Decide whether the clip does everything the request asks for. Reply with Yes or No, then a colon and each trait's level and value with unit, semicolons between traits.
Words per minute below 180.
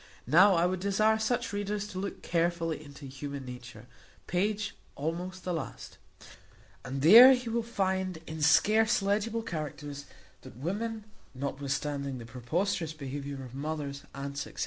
Yes: average, 145 wpm